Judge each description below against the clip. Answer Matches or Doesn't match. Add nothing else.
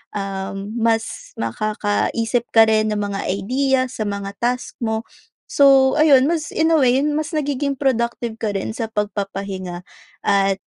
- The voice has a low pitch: Doesn't match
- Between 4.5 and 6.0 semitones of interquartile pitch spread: Matches